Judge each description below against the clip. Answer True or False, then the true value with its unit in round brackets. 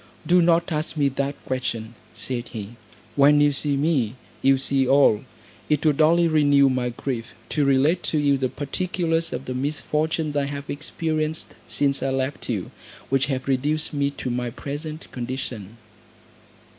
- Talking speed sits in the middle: True (160 wpm)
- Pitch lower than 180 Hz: True (140 Hz)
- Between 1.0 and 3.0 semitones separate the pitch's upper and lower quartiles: True (2.7 semitones)